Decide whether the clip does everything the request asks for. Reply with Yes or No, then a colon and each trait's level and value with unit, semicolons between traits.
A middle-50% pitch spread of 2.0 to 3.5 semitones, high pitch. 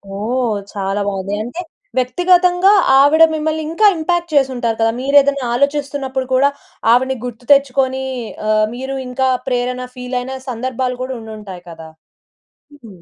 Yes: average, 3.1 semitones; very high, 260 Hz